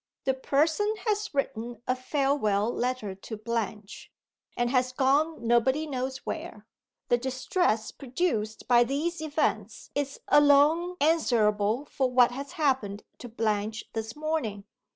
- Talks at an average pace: No, slow, 130 wpm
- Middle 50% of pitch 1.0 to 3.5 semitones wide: No, average, 4.6 semitones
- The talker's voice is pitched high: Yes, very high, 255 Hz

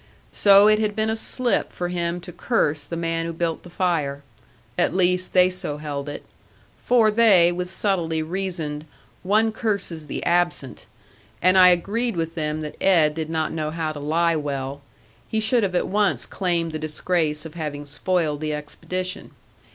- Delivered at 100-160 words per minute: No, average, 175 wpm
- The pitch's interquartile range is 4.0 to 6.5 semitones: No, average, 3.5 semitones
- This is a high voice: No, medium, 170 Hz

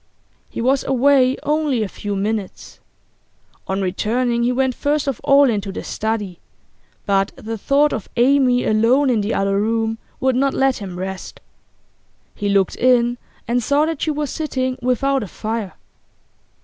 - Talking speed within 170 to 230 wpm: No, average, 160 wpm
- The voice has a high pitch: Yes, high, 240 Hz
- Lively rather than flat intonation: No, average, 4.4 semitones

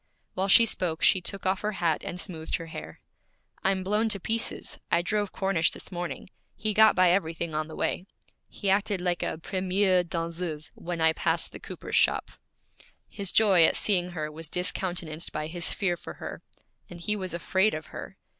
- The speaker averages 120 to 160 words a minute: No, average, 190 wpm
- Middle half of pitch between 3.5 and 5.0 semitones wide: No, average, 2.9 semitones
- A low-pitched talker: No, medium, 180 Hz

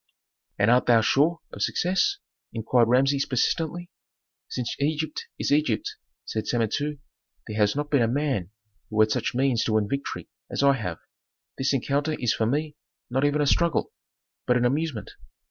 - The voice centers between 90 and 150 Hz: Yes, low, 135 Hz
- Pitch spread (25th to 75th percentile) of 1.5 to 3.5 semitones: No, average, 4.4 semitones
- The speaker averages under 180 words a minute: Yes, average, 165 wpm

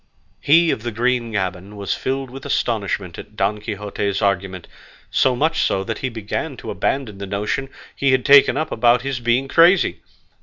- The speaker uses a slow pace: No, average, 180 wpm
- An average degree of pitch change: Yes, average, 5.0 semitones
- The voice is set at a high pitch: No, low, 115 Hz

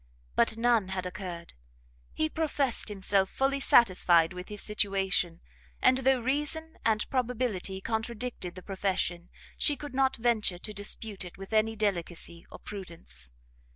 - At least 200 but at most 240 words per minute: No, average, 140 wpm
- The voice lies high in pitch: Yes, high, 210 Hz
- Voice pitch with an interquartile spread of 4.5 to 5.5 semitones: Yes, average, 5.1 semitones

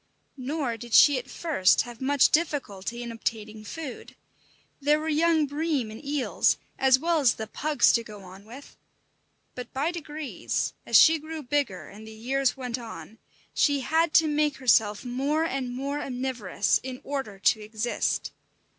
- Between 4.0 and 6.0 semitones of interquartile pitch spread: Yes, average, 4.6 semitones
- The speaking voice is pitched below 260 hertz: No, very high, 265 Hz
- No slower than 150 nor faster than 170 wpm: Yes, average, 165 wpm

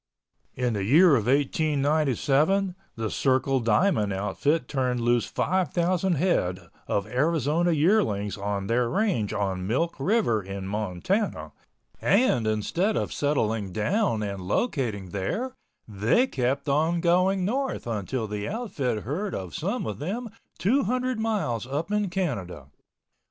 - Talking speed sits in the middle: No, slow, 130 wpm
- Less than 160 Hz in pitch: Yes, low, 135 Hz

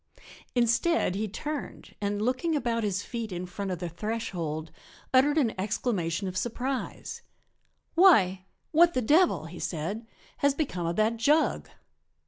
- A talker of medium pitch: No, high, 220 Hz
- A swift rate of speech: No, average, 140 wpm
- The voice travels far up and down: Yes, wide, 6.6 semitones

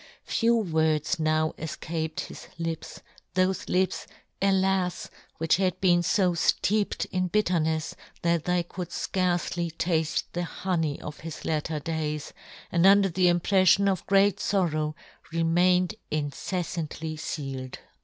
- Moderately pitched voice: Yes, medium, 170 Hz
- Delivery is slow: Yes, slow, 125 wpm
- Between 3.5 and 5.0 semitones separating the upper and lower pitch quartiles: No, average, 2.7 semitones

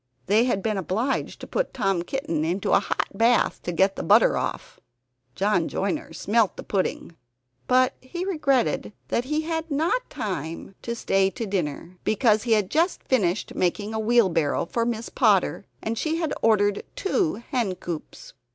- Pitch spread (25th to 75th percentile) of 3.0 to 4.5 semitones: No, wide, 5.5 semitones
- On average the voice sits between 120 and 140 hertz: No, high, 220 Hz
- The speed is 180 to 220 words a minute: No, average, 170 wpm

